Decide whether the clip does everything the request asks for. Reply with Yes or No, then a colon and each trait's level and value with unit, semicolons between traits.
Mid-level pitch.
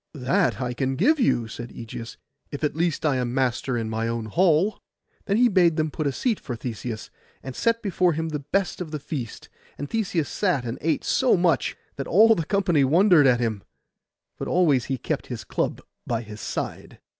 Yes: medium, 150 Hz